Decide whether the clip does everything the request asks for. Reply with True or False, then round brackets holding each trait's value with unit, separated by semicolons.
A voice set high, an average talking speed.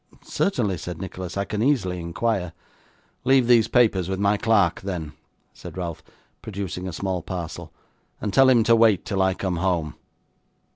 False (95 Hz; 160 wpm)